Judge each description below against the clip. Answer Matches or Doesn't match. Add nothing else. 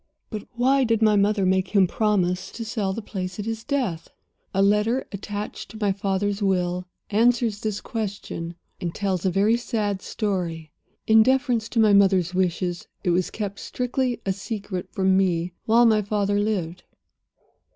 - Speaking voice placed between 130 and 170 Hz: Doesn't match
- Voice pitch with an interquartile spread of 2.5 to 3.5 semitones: Matches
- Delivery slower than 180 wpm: Matches